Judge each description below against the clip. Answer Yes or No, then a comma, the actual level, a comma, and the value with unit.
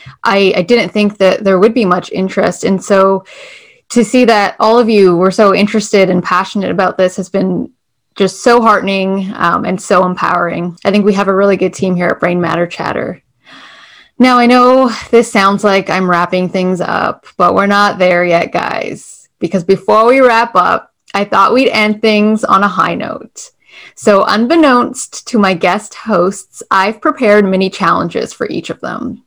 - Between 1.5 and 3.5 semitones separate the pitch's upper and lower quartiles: Yes, average, 2.9 semitones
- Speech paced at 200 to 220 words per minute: No, average, 185 wpm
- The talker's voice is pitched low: No, high, 195 Hz